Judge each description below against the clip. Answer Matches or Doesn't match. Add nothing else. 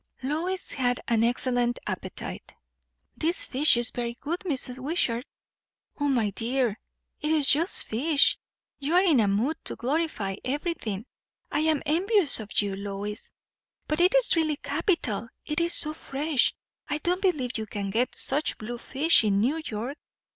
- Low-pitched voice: Doesn't match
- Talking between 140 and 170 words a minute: Matches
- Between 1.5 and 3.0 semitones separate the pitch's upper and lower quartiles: Doesn't match